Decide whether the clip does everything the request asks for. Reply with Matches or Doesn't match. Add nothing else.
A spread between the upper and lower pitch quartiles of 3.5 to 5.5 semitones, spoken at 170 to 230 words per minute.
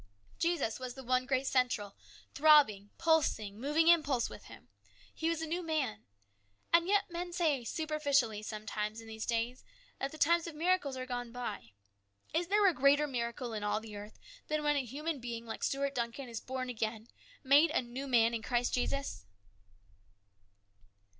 Matches